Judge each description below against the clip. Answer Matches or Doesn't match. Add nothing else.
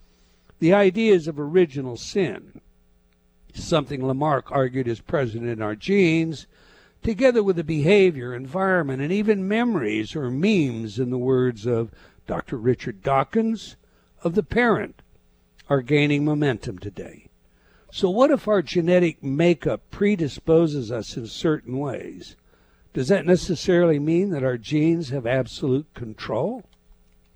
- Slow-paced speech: Matches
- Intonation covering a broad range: Matches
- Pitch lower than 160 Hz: Matches